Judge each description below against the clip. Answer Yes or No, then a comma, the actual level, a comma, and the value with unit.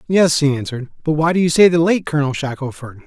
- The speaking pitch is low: No, medium, 150 Hz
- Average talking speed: No, fast, 235 wpm